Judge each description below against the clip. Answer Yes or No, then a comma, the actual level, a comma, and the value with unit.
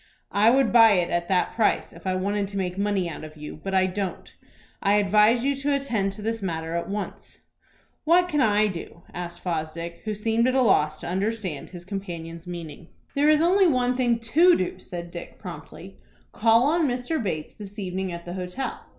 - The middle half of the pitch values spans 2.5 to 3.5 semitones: No, average, 5.1 semitones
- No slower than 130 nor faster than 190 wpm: No, average, 200 wpm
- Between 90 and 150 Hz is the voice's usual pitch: No, high, 200 Hz